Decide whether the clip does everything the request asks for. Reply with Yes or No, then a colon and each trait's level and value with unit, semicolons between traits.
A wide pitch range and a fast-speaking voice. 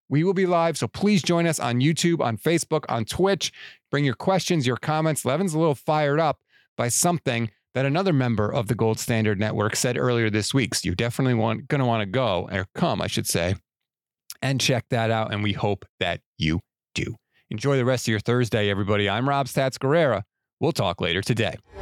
Yes: wide, 5.7 semitones; fast, 210 wpm